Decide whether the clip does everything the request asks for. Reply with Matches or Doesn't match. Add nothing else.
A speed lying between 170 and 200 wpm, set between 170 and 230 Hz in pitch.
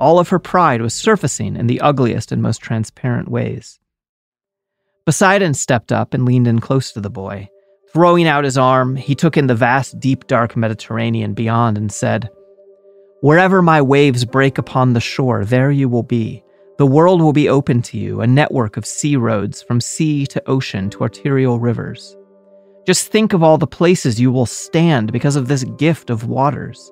Doesn't match